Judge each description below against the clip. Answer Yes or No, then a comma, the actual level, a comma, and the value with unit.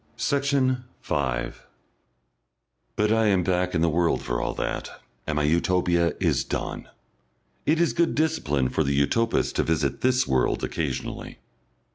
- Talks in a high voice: No, very low, 90 Hz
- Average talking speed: Yes, average, 145 wpm